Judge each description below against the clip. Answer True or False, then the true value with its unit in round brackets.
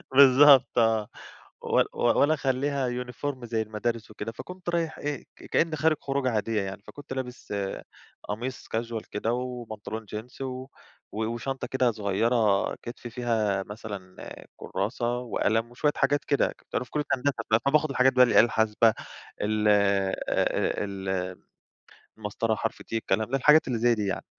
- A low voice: True (120 Hz)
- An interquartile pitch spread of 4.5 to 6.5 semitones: False (3.5 semitones)